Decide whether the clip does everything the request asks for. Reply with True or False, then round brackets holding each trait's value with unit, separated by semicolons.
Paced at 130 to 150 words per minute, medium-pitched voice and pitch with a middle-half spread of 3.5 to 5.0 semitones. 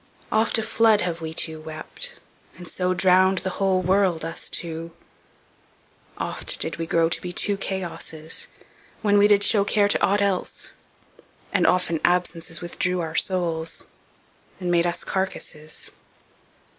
False (145 wpm; 180 Hz; 2.9 semitones)